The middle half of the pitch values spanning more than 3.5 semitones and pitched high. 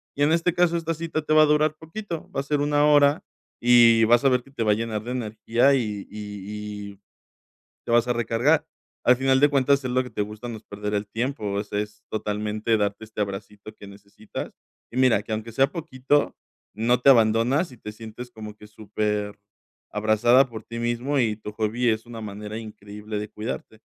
No: average, 4.2 semitones; low, 115 Hz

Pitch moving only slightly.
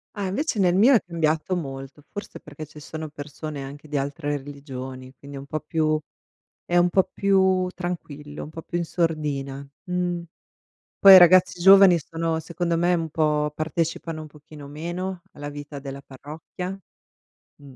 No: average, 3.4 semitones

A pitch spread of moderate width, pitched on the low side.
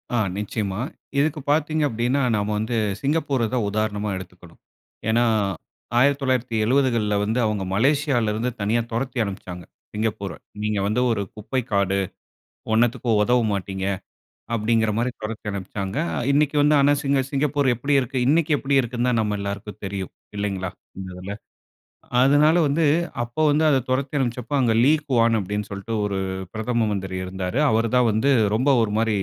Yes: average, 4.5 semitones; low, 115 Hz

